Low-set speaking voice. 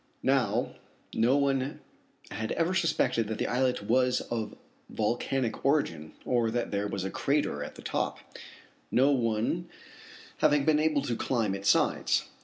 Yes: low, 125 Hz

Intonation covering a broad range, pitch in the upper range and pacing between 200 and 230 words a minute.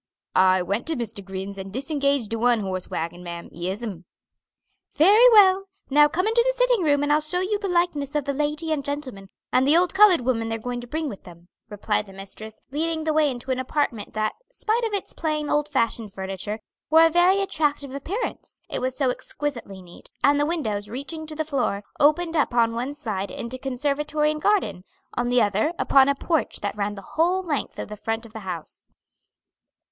Yes: wide, 6.7 semitones; very high, 275 Hz; fast, 205 wpm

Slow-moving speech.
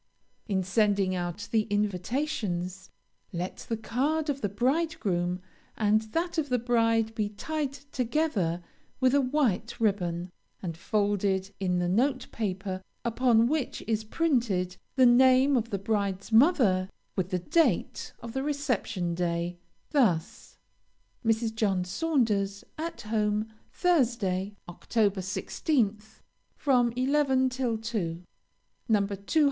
Yes: slow, 120 wpm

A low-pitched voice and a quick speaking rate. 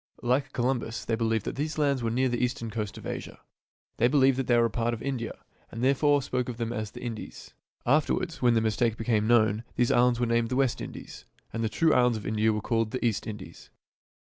Yes: low, 120 Hz; fast, 230 wpm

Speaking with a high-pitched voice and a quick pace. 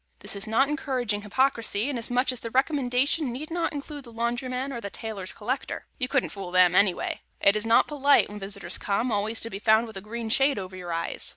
Yes: high, 230 Hz; fast, 215 wpm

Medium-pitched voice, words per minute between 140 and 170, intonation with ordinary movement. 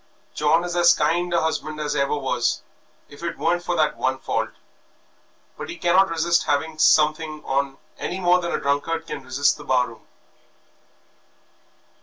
Yes: medium, 155 Hz; average, 165 wpm; average, 3.2 semitones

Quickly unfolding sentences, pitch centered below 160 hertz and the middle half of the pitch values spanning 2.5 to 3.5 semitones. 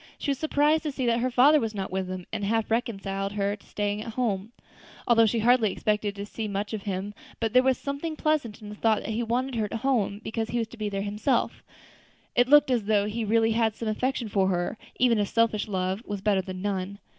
No: fast, 250 wpm; high, 220 Hz; average, 3.1 semitones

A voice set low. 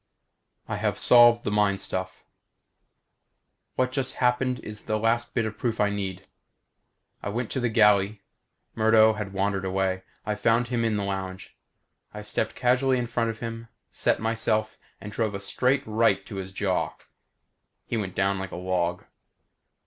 Yes: low, 110 Hz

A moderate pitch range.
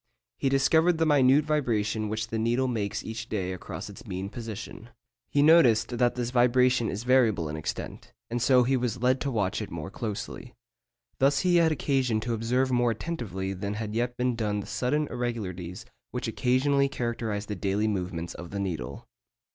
Yes: average, 3.8 semitones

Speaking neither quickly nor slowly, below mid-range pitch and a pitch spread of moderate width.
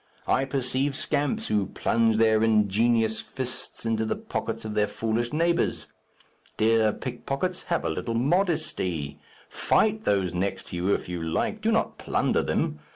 Yes: average, 155 wpm; low, 115 Hz; average, 4.6 semitones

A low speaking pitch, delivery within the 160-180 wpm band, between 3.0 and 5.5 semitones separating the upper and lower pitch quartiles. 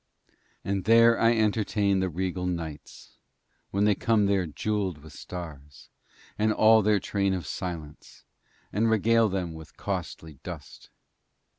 No: very low, 95 Hz; slow, 135 wpm; average, 4.1 semitones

